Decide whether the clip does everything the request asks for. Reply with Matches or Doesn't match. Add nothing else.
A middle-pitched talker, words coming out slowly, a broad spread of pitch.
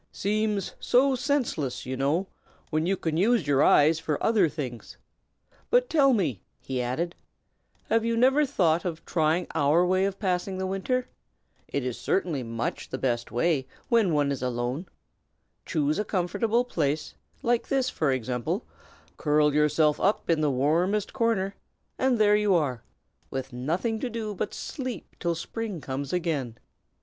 Doesn't match